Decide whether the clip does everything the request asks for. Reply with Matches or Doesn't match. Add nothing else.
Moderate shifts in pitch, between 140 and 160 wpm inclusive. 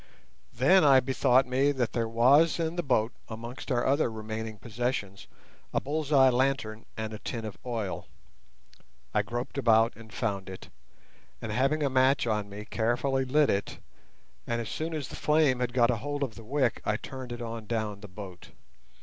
Doesn't match